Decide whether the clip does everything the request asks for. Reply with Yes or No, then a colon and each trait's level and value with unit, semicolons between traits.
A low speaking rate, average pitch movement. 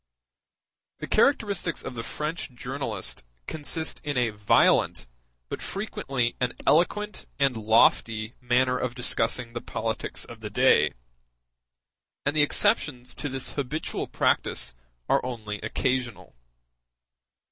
Yes: slow, 115 wpm; average, 4.1 semitones